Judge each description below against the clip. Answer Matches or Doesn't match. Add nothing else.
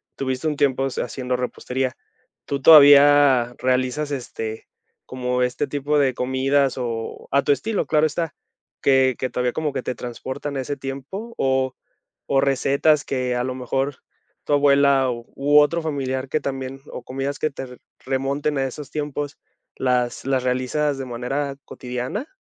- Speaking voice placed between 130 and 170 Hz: Matches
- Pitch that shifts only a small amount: Matches